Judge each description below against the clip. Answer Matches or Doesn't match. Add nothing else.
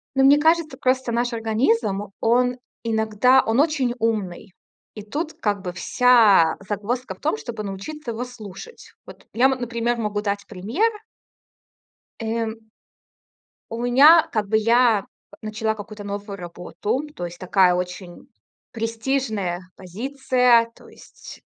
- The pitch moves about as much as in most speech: Matches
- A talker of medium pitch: Doesn't match